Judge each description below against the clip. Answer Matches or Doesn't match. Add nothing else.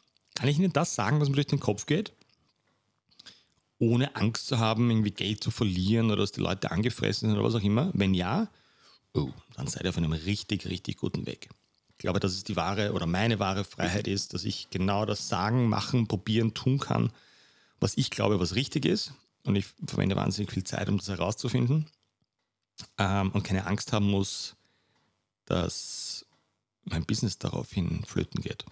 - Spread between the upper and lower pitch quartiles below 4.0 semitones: Matches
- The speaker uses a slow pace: Doesn't match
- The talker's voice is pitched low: Matches